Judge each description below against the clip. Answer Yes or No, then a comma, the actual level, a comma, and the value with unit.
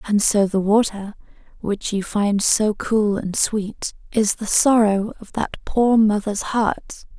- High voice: Yes, high, 210 Hz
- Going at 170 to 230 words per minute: No, average, 160 wpm